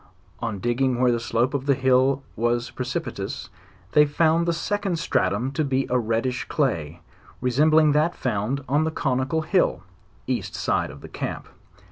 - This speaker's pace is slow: No, average, 160 wpm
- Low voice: Yes, low, 130 Hz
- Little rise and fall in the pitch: No, average, 4.0 semitones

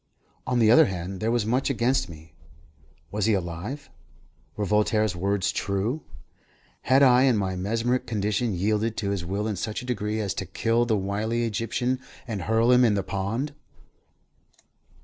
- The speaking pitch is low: Yes, low, 110 Hz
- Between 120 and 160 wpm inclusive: No, average, 170 wpm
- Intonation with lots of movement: No, average, 3.3 semitones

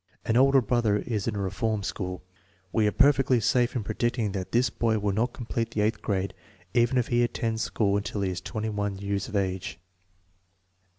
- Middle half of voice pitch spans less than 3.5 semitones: Yes, average, 3.1 semitones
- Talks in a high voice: No, low, 110 Hz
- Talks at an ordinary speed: Yes, average, 190 wpm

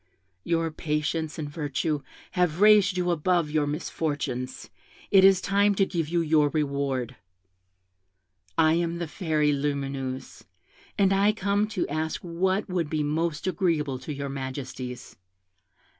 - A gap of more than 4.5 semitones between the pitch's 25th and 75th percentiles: No, average, 3.8 semitones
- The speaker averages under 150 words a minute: Yes, slow, 135 wpm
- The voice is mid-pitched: Yes, medium, 160 Hz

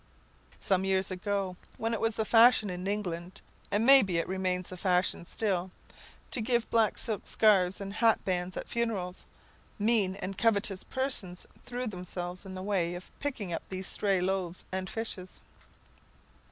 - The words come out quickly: No, average, 160 wpm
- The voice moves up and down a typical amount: Yes, average, 3.2 semitones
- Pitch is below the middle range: No, high, 195 Hz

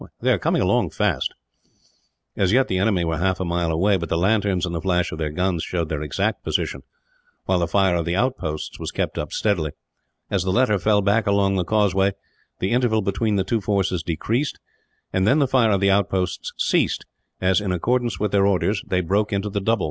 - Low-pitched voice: Yes, very low, 95 Hz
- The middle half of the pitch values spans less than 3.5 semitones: Yes, average, 2.9 semitones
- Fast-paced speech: Yes, fast, 215 wpm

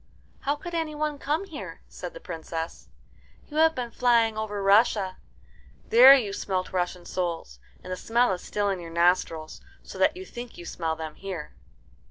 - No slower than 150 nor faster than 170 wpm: No, average, 180 wpm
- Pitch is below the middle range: No, high, 205 Hz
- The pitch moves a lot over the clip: Yes, wide, 7.1 semitones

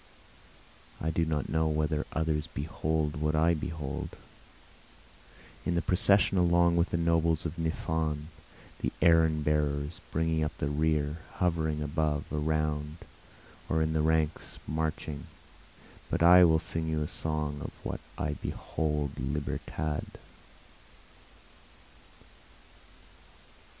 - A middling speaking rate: No, slow, 115 wpm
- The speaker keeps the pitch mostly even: Yes, narrow, 1.2 semitones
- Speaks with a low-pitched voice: Yes, very low, 80 Hz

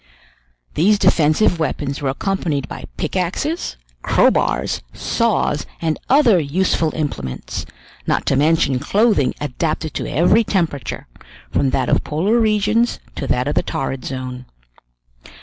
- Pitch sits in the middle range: Yes, medium, 160 Hz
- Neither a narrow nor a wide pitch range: No, wide, 6.5 semitones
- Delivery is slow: Yes, slow, 125 wpm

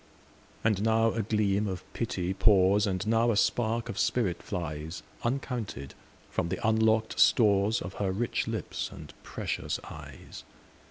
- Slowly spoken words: Yes, slow, 125 wpm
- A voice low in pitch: Yes, low, 105 Hz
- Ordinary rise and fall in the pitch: Yes, average, 3.0 semitones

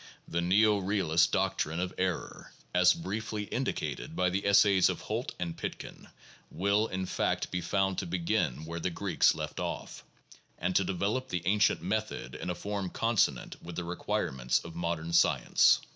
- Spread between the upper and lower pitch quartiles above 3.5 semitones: No, average, 3.2 semitones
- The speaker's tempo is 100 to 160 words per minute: No, average, 170 wpm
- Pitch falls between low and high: No, very low, 90 Hz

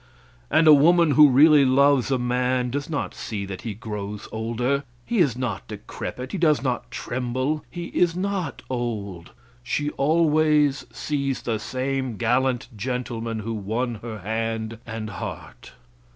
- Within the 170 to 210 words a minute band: No, average, 150 wpm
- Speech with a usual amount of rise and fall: Yes, average, 4.3 semitones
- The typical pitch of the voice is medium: No, low, 125 Hz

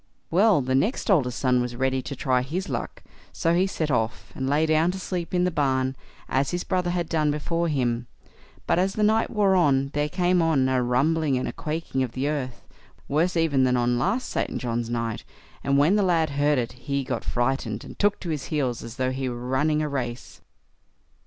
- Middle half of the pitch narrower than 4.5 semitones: No, average, 4.8 semitones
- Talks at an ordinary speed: No, fast, 215 wpm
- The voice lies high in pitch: No, medium, 140 Hz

